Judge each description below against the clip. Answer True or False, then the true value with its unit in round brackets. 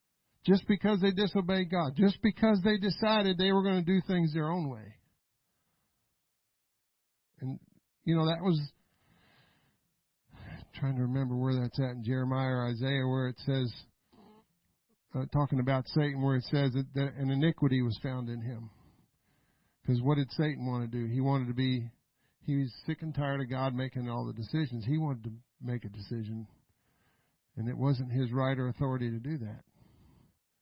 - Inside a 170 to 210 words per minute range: True (175 wpm)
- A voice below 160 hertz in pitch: True (135 Hz)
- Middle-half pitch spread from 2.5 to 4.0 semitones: False (4.4 semitones)